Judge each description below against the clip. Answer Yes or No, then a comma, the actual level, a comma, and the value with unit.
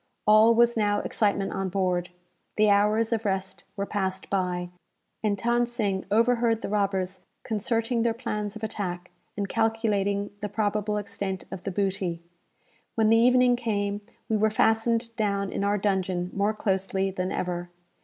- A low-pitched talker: No, high, 205 Hz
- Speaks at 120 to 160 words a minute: Yes, average, 155 wpm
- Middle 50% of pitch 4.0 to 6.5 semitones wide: No, narrow, 2.6 semitones